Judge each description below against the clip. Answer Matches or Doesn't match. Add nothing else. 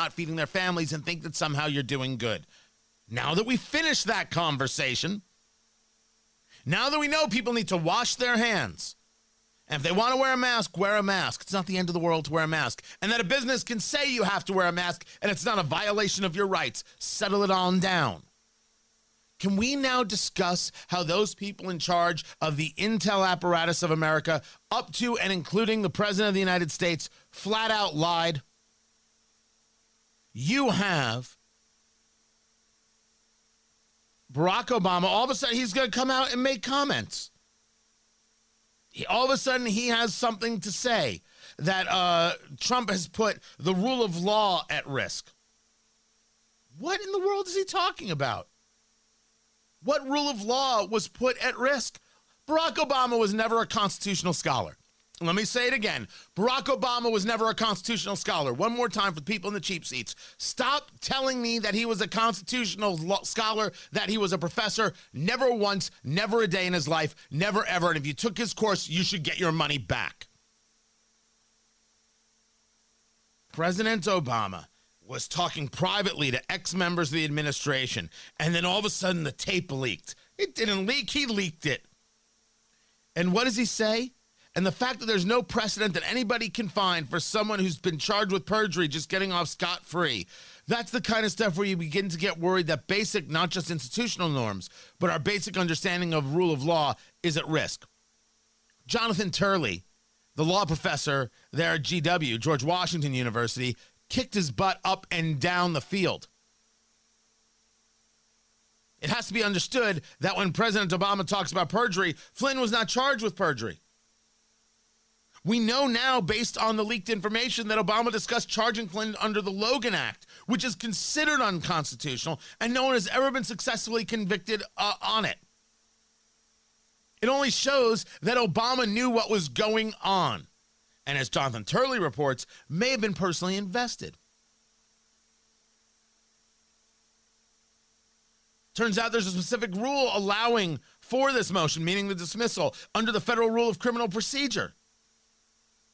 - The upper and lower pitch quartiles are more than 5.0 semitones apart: Matches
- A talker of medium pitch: Doesn't match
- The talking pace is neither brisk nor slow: Matches